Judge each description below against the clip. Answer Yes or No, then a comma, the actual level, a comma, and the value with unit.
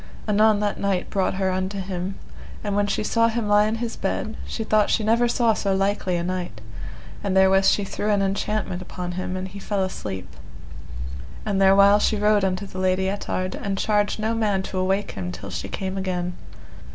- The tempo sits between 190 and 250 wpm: Yes, average, 200 wpm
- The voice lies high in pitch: Yes, high, 195 Hz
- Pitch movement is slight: Yes, narrow, 2.0 semitones